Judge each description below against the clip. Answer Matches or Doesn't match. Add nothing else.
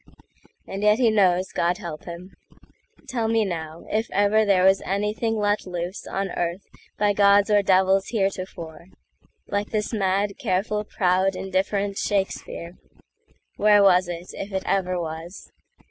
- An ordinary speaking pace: Doesn't match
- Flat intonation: Matches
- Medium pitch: Doesn't match